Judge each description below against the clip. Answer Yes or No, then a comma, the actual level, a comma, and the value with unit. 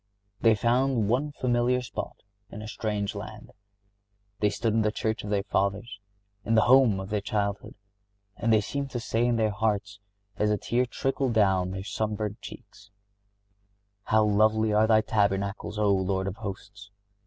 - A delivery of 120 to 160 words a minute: No, average, 170 wpm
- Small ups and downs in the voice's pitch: Yes, narrow, 2.1 semitones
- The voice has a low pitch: Yes, low, 105 Hz